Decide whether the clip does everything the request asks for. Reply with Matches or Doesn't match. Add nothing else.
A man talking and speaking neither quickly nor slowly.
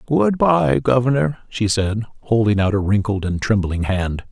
Matches